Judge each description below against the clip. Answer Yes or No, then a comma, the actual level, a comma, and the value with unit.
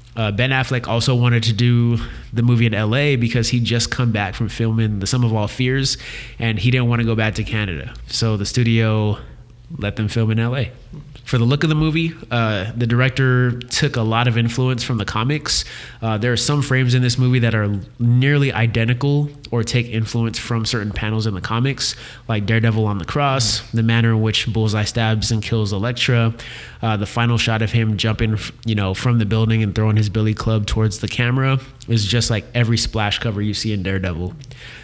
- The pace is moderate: No, fast, 210 wpm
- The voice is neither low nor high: No, low, 115 Hz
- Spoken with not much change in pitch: Yes, narrow, 2.1 semitones